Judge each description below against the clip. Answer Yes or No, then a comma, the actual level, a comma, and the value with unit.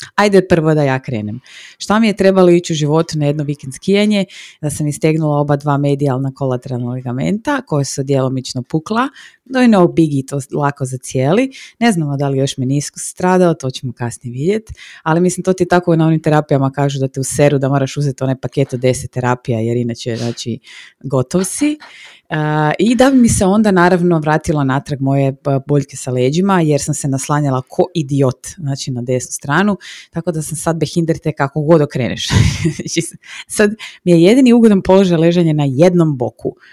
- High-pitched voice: No, medium, 150 Hz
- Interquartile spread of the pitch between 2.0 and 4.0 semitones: No, average, 4.7 semitones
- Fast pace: Yes, fast, 185 wpm